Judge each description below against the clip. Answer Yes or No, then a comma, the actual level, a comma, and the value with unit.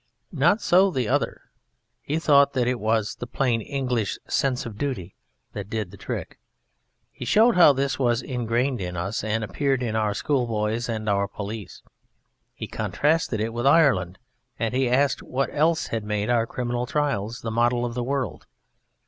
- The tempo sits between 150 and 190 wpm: Yes, average, 175 wpm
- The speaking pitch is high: No, low, 120 Hz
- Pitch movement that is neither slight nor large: Yes, average, 4.1 semitones